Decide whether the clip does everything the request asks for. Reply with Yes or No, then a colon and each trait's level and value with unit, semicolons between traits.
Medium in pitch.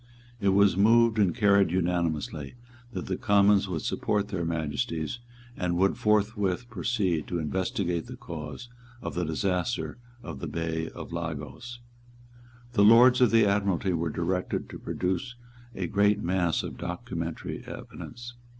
No: very low, 95 Hz